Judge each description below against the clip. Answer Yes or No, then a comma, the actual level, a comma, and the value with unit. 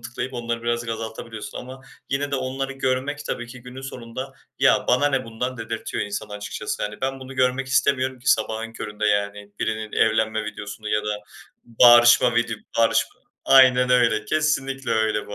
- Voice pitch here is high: No, low, 120 Hz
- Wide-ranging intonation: No, average, 3.0 semitones